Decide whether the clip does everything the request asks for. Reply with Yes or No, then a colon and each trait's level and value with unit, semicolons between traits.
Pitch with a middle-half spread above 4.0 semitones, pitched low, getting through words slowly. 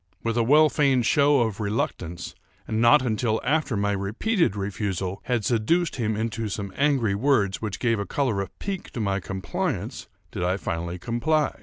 No: average, 5.2 semitones; low, 110 Hz; average, 175 wpm